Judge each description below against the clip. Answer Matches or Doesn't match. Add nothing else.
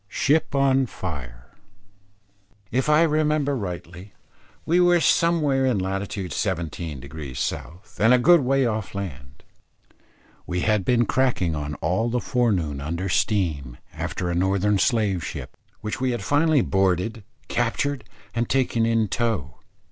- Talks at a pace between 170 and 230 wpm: Doesn't match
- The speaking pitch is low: Matches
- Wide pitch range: Matches